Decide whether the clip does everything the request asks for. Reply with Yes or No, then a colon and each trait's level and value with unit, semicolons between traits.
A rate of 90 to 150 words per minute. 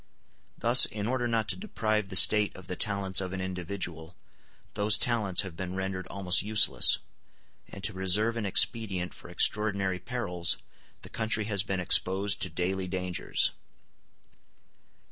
Yes: average, 145 wpm